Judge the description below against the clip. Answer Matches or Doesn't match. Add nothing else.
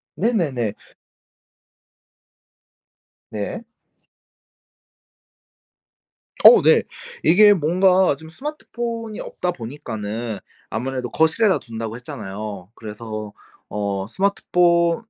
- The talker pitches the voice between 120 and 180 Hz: Matches